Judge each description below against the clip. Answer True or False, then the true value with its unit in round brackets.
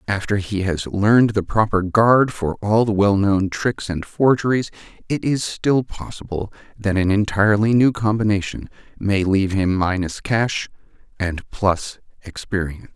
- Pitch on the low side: True (100 Hz)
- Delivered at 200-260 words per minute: False (145 wpm)